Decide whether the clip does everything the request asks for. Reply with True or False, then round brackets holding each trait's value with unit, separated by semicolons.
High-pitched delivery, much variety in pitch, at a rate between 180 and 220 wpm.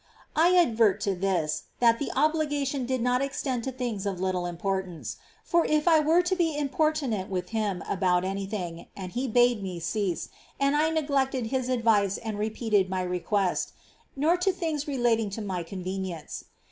True (225 Hz; 6.8 semitones; 185 wpm)